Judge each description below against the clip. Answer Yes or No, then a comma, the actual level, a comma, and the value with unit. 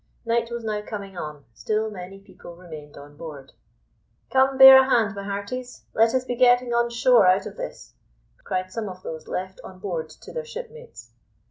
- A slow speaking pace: No, average, 190 wpm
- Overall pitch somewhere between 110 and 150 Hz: No, high, 210 Hz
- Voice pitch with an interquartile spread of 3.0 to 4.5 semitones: No, average, 5.0 semitones